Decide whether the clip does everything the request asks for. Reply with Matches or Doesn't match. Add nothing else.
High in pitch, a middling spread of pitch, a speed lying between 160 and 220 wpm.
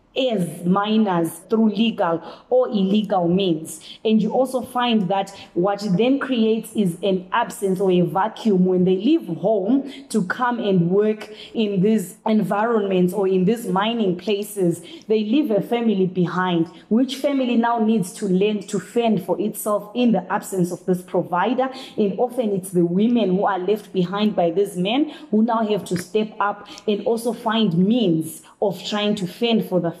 Matches